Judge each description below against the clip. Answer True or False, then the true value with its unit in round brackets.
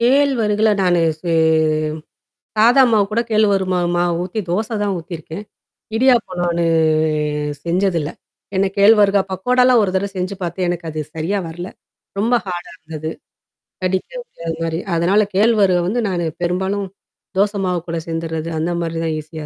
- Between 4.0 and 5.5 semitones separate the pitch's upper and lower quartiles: False (3.6 semitones)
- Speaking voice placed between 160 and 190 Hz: True (185 Hz)